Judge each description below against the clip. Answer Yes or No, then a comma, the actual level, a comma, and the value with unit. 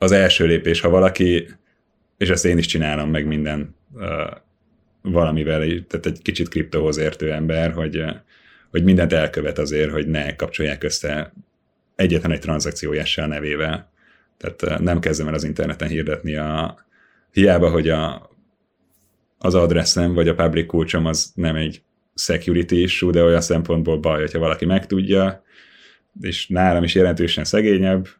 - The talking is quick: No, average, 140 wpm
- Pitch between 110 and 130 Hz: No, very low, 85 Hz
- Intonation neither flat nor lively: No, narrow, 2.1 semitones